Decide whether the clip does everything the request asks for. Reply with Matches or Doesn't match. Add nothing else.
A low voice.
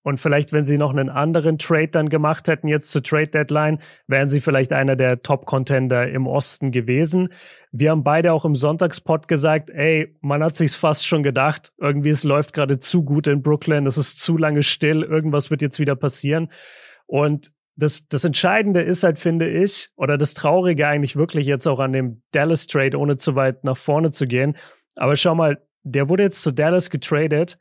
Doesn't match